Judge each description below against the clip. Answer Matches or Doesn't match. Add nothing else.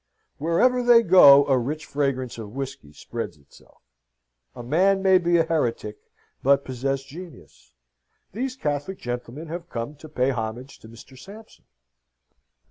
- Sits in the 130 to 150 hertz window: Matches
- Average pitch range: Doesn't match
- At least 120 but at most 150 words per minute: Matches